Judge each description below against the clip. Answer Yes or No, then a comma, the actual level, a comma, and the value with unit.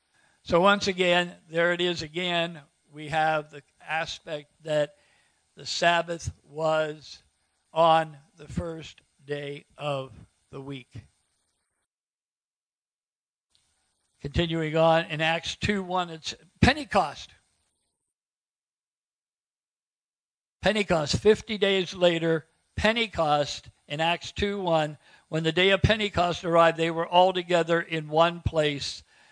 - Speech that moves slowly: Yes, slow, 100 wpm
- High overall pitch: No, medium, 160 Hz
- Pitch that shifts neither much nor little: Yes, average, 3.3 semitones